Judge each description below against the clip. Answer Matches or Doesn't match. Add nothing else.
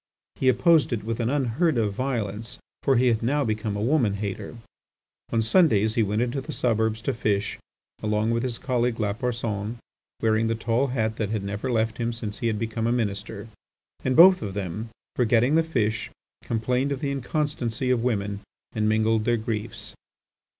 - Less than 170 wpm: Doesn't match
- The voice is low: Matches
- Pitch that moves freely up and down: Doesn't match